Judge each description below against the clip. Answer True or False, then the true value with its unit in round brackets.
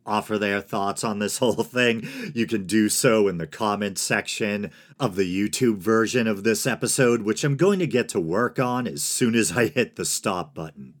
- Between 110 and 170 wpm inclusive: False (205 wpm)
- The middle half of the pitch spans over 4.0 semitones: False (3.1 semitones)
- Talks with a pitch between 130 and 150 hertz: False (110 Hz)